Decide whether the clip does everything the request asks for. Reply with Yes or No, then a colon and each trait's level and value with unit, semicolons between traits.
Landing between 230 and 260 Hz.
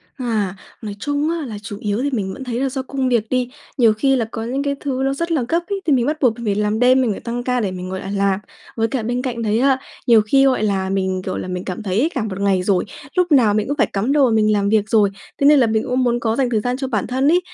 Yes: high, 235 Hz